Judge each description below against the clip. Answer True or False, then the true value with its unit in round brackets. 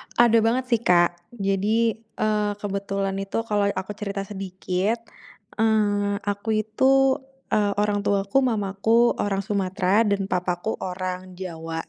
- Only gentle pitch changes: True (2.3 semitones)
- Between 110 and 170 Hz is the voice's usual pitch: False (200 Hz)